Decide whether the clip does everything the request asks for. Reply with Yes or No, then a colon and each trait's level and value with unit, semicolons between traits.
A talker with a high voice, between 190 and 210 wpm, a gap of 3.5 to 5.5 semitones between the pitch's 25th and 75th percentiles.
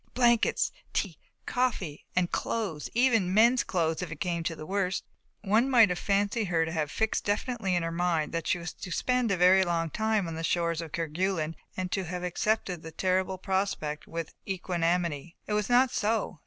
No: medium, 180 Hz; average, 195 wpm; average, 4.0 semitones